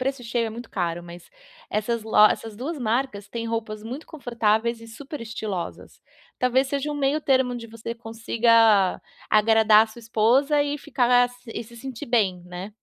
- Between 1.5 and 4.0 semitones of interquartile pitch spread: Yes, average, 2.7 semitones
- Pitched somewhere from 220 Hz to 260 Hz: Yes, high, 230 Hz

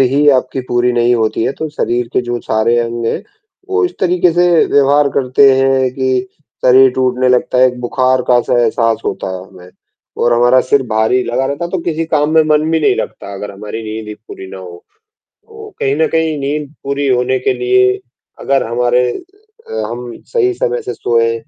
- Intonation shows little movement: No, average, 3.7 semitones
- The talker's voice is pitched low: Yes, low, 130 Hz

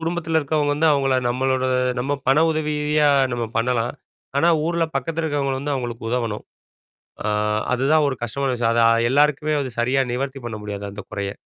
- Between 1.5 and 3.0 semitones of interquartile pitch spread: No, average, 3.7 semitones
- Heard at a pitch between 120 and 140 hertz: Yes, low, 135 Hz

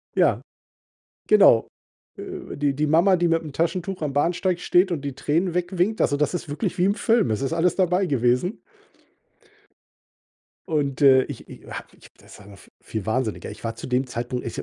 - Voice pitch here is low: No, medium, 155 Hz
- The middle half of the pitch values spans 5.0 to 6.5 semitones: Yes, wide, 5.4 semitones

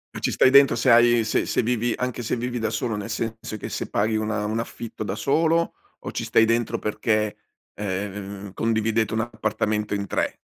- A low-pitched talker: Yes, low, 110 Hz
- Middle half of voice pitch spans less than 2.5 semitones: Yes, narrow, 2.0 semitones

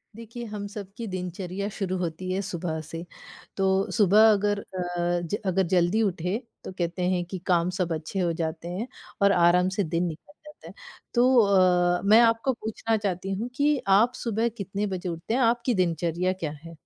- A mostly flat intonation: No, average, 3.4 semitones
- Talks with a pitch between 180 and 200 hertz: Yes, high, 190 Hz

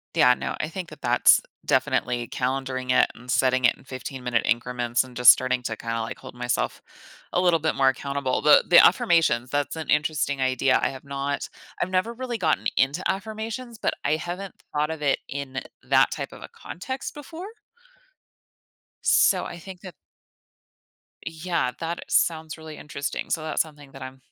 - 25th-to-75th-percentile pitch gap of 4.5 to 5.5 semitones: Yes, average, 4.9 semitones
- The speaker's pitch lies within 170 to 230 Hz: No, medium, 145 Hz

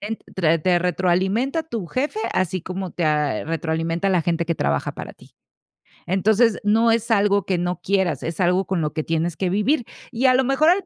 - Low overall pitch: No, medium, 185 Hz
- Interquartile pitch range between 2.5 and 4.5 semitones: No, average, 5.0 semitones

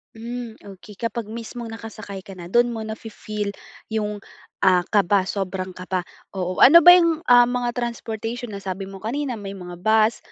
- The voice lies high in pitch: Yes, high, 220 Hz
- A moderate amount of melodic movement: Yes, average, 3.5 semitones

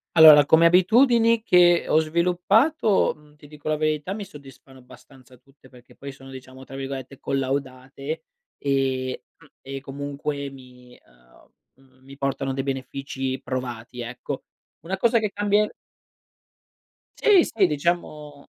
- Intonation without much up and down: No, average, 4.4 semitones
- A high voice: No, medium, 140 Hz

